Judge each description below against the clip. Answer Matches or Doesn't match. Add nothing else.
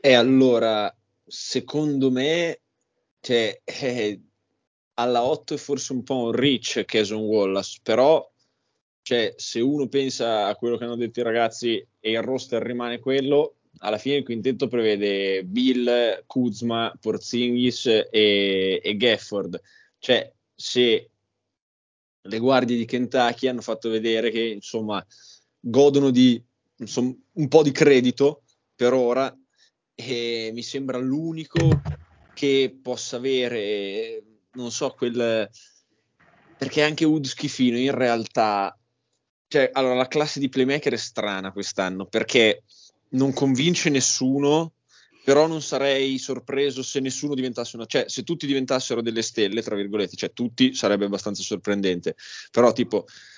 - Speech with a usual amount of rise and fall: Matches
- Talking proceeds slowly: Doesn't match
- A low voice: Matches